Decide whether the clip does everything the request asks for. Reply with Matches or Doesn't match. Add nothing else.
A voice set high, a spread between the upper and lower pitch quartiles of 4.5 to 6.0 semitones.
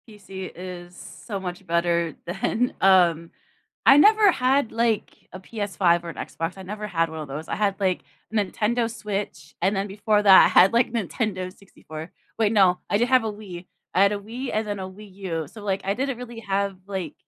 Doesn't match